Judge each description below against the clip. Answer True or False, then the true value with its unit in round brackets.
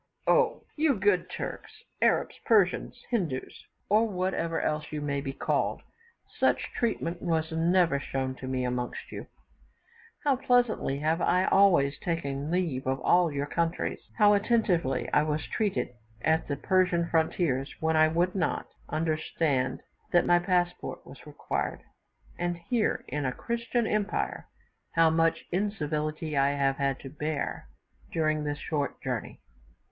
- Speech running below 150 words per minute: True (140 wpm)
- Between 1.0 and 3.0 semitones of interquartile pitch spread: False (4.3 semitones)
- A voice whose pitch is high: False (165 Hz)